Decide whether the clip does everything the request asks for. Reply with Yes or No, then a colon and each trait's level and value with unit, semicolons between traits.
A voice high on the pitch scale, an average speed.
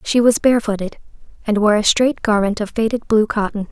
Yes: high, 220 Hz; average, 195 wpm